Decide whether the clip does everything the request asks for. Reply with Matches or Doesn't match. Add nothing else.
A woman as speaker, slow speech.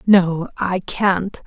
Matches